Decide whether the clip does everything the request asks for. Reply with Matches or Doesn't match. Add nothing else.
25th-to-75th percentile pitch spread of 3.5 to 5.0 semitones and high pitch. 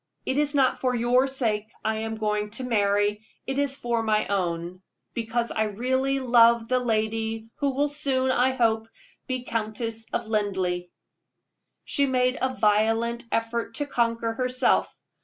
Doesn't match